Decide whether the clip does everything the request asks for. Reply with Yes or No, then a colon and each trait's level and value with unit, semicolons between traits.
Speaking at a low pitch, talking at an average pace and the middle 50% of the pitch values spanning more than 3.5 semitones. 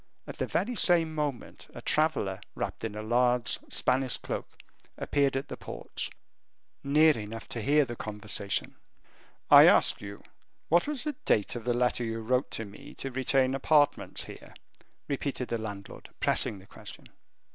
Yes: low, 125 Hz; average, 160 wpm; average, 4.6 semitones